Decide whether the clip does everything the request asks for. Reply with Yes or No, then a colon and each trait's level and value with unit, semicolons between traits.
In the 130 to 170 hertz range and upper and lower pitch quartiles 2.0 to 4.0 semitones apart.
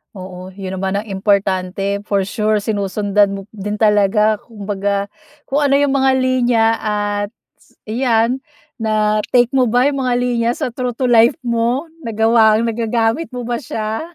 No: high, 220 Hz; average, 3.1 semitones